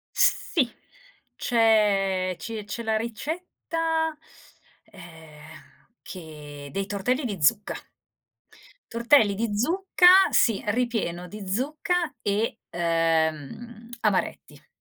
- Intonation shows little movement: No, wide, 5.6 semitones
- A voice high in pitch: Yes, high, 215 Hz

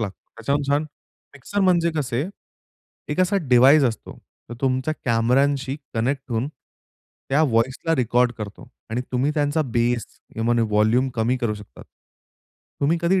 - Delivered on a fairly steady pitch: No, average, 3.8 semitones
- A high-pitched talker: No, low, 130 Hz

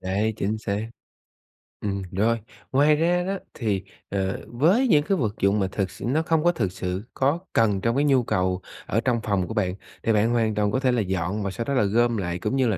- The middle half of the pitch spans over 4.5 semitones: Yes, average, 5.1 semitones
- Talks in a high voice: No, low, 110 Hz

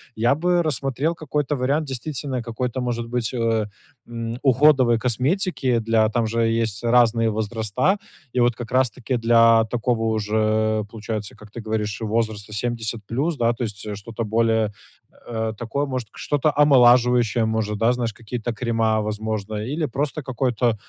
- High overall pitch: No, low, 115 Hz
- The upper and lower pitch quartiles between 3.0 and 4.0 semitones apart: No, narrow, 2.5 semitones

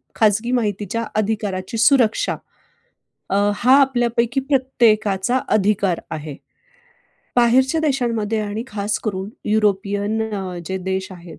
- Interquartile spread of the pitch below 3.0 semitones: No, average, 3.4 semitones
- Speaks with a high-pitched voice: Yes, high, 215 Hz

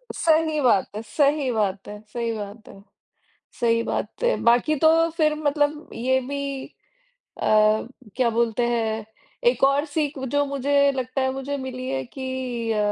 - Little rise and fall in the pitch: No, average, 3.7 semitones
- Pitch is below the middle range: No, very high, 260 Hz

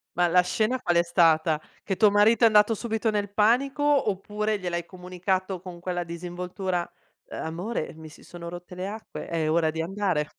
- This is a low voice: No, medium, 180 Hz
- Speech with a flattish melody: No, average, 3.5 semitones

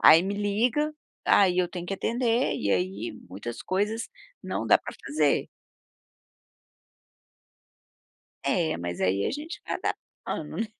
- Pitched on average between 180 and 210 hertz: Yes, high, 190 Hz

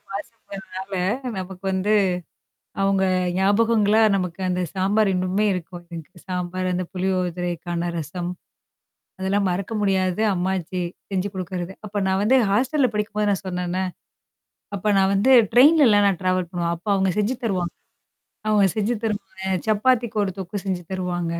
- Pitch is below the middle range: No, high, 190 Hz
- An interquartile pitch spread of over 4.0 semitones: No, narrow, 2.4 semitones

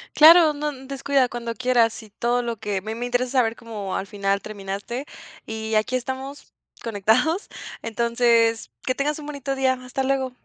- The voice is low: No, high, 245 Hz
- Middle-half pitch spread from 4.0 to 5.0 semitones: No, average, 3.2 semitones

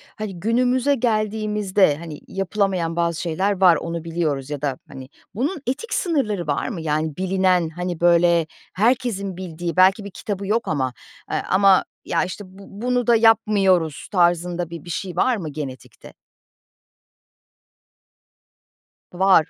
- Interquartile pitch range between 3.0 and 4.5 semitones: Yes, average, 4.1 semitones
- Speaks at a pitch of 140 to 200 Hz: Yes, medium, 185 Hz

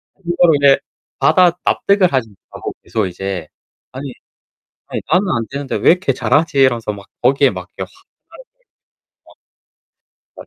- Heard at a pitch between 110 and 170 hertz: Yes, low, 135 Hz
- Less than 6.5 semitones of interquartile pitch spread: No, wide, 7.6 semitones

